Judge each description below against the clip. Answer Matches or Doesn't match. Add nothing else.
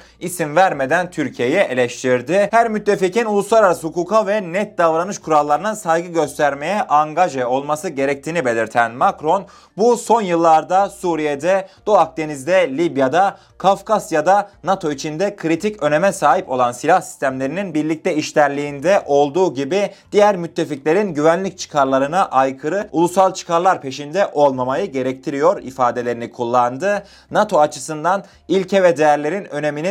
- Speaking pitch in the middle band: Matches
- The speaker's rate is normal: Matches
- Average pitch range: Matches